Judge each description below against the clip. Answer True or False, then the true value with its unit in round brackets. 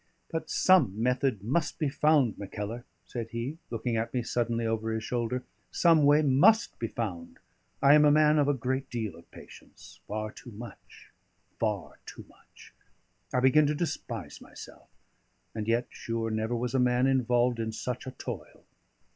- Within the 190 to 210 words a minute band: False (170 wpm)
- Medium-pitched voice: False (120 Hz)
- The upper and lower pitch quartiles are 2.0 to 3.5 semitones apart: False (3.9 semitones)